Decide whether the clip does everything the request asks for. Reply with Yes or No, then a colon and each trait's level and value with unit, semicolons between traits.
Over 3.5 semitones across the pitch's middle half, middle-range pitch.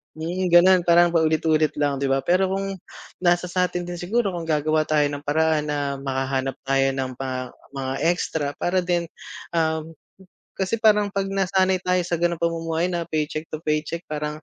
No: average, 3.2 semitones; medium, 165 Hz